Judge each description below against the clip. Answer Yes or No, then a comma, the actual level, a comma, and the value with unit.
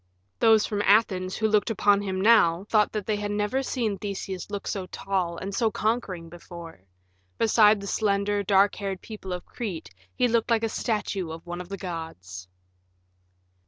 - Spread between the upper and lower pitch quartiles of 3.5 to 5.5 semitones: No, average, 2.9 semitones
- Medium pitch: No, high, 200 Hz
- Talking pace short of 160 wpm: No, average, 175 wpm